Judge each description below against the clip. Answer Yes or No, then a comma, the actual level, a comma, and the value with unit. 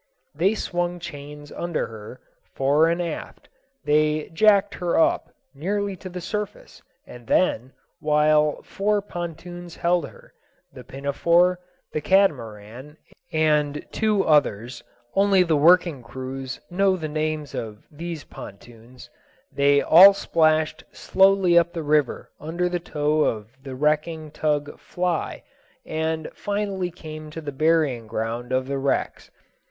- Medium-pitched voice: Yes, medium, 155 Hz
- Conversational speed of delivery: No, slow, 125 wpm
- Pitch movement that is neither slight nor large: Yes, average, 3.8 semitones